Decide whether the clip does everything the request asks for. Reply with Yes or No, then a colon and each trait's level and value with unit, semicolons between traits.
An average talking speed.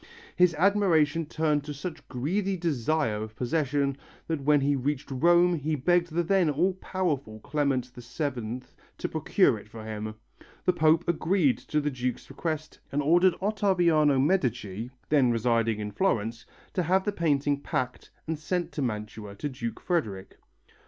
Yes: average, 155 wpm